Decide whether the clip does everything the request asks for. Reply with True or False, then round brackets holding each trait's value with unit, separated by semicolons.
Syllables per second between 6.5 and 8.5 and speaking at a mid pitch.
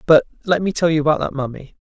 True (6.8 syllables/s; 155 Hz)